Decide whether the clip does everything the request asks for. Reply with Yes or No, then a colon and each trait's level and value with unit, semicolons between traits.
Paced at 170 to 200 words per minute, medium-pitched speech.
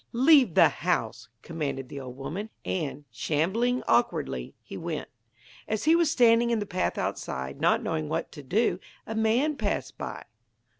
No: average, 160 wpm; medium, 180 Hz